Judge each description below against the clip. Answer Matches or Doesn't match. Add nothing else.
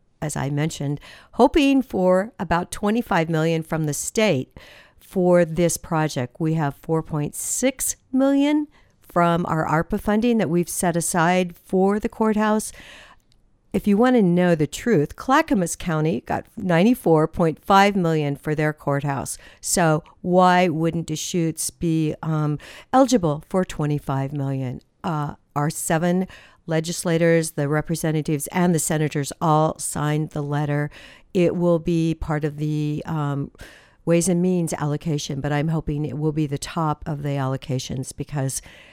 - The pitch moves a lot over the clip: Doesn't match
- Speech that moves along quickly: Doesn't match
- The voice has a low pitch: Doesn't match